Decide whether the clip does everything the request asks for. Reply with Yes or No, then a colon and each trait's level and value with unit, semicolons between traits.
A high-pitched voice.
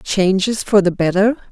Yes: high, 200 Hz